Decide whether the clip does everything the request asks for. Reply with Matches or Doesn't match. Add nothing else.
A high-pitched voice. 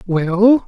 Matches